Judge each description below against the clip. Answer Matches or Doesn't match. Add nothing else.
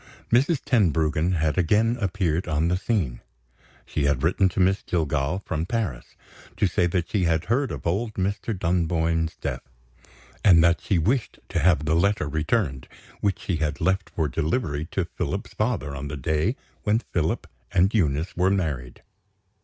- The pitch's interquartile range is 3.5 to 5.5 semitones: Matches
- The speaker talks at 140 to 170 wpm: Matches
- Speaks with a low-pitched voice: Matches